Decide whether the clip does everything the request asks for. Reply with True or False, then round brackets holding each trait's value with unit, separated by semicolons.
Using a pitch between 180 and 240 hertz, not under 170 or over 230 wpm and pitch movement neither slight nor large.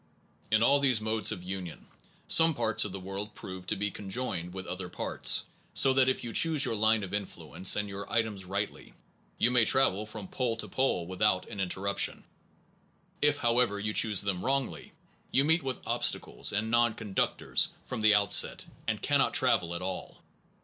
False (105 Hz; 185 wpm; 3.7 semitones)